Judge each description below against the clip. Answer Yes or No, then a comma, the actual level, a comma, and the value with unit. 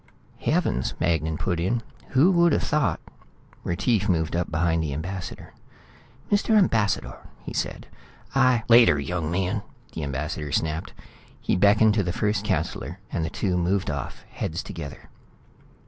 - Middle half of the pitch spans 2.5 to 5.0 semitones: No, wide, 5.6 semitones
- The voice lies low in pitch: Yes, very low, 90 Hz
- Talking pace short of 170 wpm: Yes, average, 150 wpm